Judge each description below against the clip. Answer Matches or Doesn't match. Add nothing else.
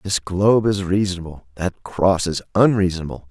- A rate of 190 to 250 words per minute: Doesn't match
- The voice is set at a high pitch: Doesn't match